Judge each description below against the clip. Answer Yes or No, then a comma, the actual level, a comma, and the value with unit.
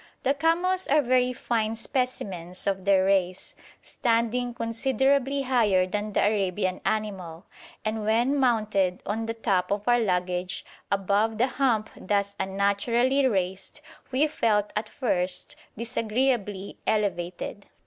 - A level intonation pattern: No, average, 4.2 semitones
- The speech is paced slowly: Yes, slow, 125 wpm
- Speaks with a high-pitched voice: Yes, high, 215 Hz